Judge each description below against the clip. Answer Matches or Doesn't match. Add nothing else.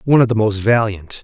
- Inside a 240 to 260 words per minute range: Matches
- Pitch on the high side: Doesn't match